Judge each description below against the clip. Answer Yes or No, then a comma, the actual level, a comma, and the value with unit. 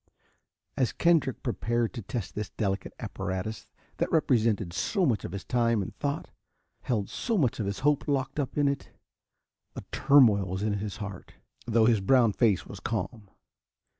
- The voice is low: Yes, low, 115 Hz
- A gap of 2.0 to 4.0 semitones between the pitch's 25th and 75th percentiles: No, average, 4.7 semitones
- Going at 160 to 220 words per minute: Yes, average, 165 wpm